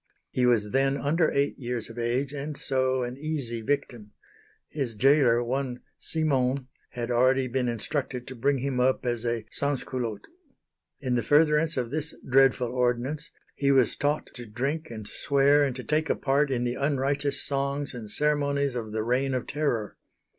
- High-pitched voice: No, low, 130 Hz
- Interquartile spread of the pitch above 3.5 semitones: No, average, 2.7 semitones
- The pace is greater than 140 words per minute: Yes, average, 170 wpm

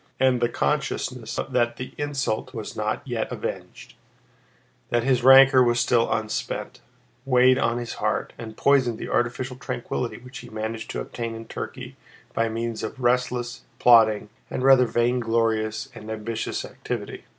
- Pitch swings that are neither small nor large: No, narrow, 2.0 semitones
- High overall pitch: No, low, 120 Hz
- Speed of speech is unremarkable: Yes, average, 150 wpm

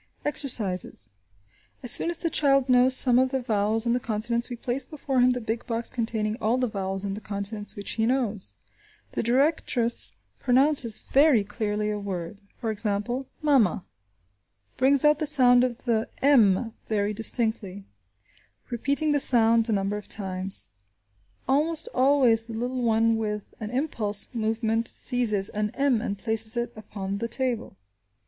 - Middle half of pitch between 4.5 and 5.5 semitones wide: No, average, 3.4 semitones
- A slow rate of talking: No, average, 160 wpm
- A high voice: Yes, high, 230 Hz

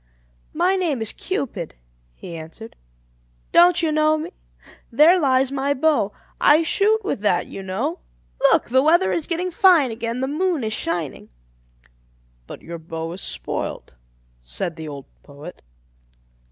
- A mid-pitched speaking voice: No, very high, 265 Hz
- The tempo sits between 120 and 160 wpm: Yes, average, 145 wpm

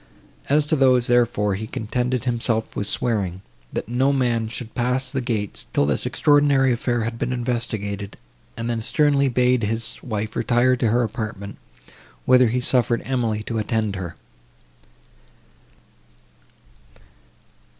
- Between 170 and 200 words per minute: No, slow, 135 wpm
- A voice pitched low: Yes, low, 120 Hz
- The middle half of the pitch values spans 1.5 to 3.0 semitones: Yes, average, 2.7 semitones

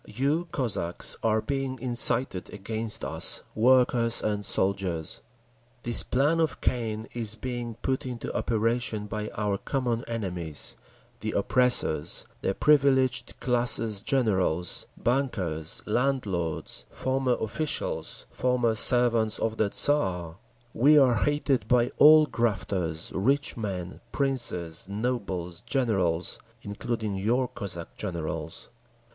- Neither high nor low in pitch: No, low, 115 Hz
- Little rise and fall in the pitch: No, average, 4.6 semitones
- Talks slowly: Yes, slow, 105 wpm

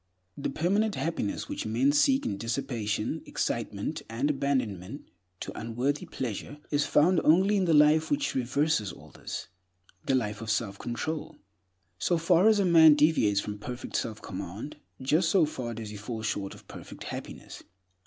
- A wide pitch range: Yes, wide, 6.4 semitones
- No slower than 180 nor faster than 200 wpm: No, average, 165 wpm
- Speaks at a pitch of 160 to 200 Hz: No, medium, 140 Hz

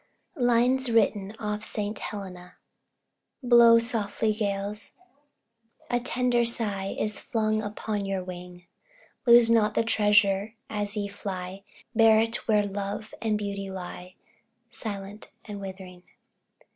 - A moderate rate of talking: No, slow, 120 wpm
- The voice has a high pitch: Yes, high, 210 Hz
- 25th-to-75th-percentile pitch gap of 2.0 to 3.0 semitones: Yes, narrow, 2.4 semitones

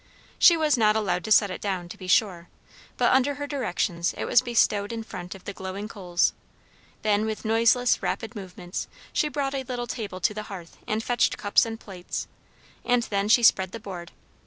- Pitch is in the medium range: No, high, 215 Hz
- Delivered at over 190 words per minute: Yes, average, 200 wpm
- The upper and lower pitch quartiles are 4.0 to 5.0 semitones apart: Yes, average, 4.3 semitones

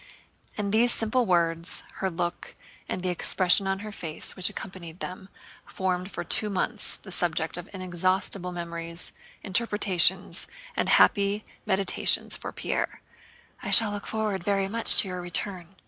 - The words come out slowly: No, average, 145 wpm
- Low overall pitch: No, high, 190 Hz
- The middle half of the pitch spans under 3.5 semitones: Yes, narrow, 2.5 semitones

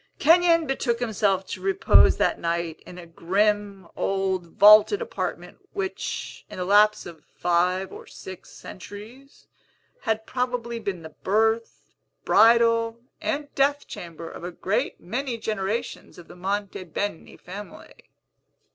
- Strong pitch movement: No, average, 4.3 semitones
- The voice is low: No, high, 210 Hz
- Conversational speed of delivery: No, slow, 130 wpm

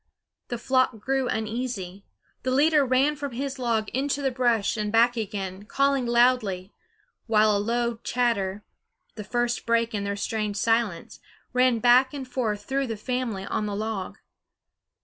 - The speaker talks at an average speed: Yes, average, 155 wpm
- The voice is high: Yes, high, 235 Hz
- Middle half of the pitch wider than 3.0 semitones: Yes, average, 3.4 semitones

